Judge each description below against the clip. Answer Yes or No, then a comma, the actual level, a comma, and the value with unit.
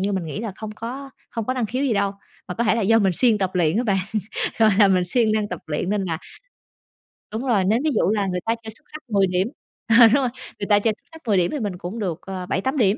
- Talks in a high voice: Yes, high, 210 Hz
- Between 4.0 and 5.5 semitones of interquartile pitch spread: No, average, 3.3 semitones